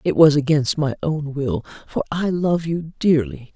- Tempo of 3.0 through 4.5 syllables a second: Yes, 4.2 syllables/s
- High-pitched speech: No, medium, 145 Hz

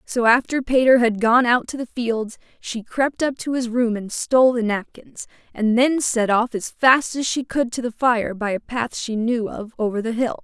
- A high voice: Yes, high, 235 Hz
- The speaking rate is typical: No, fast, 230 wpm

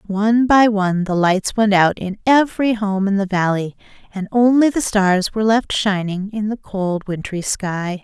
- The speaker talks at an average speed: Yes, average, 185 wpm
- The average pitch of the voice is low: No, high, 205 Hz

